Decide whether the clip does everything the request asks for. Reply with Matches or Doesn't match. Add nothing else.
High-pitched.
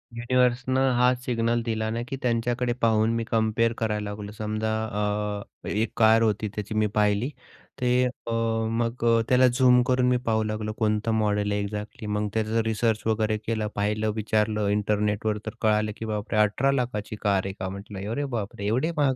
Doesn't match